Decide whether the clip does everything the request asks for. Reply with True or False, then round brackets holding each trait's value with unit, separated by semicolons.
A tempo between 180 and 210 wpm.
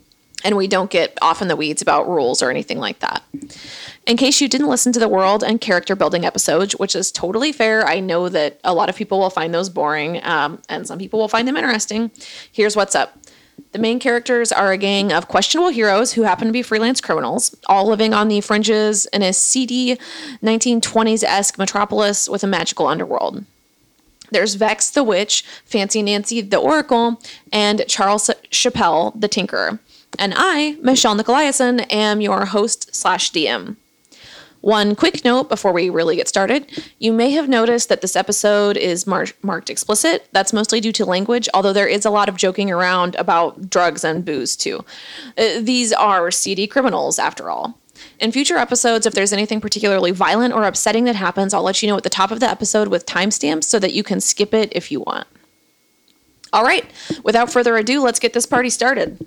True (190 wpm)